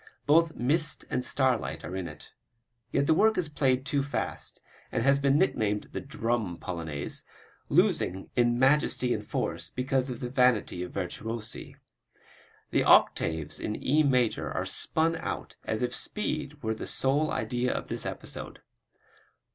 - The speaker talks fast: No, average, 155 wpm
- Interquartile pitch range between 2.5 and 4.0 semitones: No, average, 4.6 semitones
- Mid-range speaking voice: No, low, 125 Hz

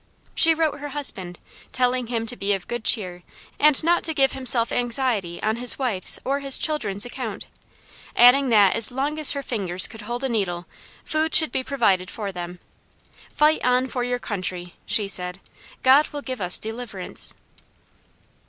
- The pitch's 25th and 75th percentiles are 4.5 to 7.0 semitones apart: Yes, wide, 5.5 semitones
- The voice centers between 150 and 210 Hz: No, high, 245 Hz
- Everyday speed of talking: Yes, average, 170 wpm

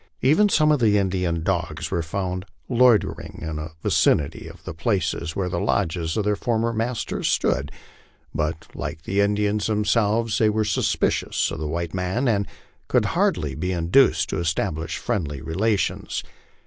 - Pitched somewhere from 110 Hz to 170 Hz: No, very low, 95 Hz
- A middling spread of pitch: Yes, average, 5.0 semitones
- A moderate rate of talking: Yes, average, 160 wpm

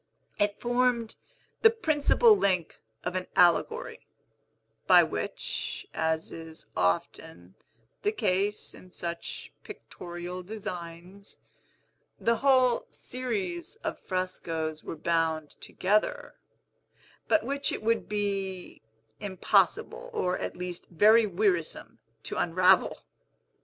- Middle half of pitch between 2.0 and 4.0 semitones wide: No, average, 5.2 semitones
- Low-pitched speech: No, medium, 185 Hz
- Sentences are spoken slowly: Yes, slow, 100 wpm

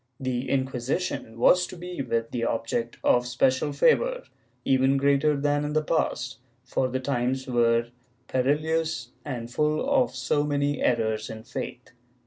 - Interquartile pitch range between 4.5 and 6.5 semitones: No, average, 3.2 semitones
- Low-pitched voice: Yes, low, 130 Hz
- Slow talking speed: No, average, 145 wpm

